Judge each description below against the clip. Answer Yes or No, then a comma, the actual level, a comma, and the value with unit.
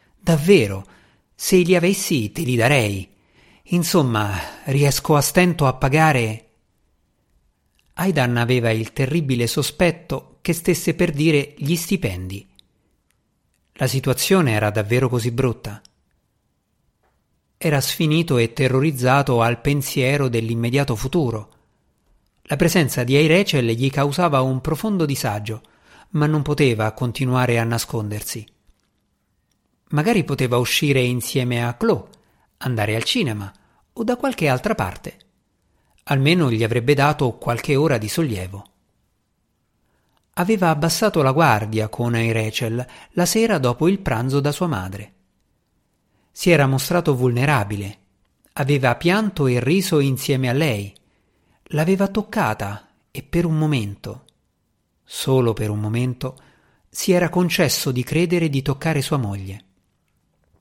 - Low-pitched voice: Yes, low, 130 Hz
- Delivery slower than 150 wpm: Yes, average, 120 wpm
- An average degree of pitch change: No, wide, 6.3 semitones